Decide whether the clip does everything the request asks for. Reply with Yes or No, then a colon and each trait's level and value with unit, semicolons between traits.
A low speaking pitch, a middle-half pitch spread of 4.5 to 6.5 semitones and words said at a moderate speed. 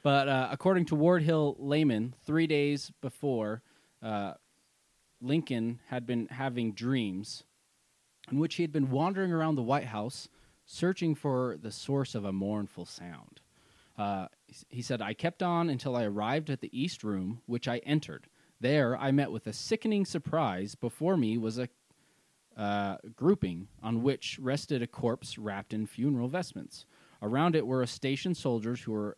Yes: low, 130 Hz; average, 5.3 semitones; average, 165 wpm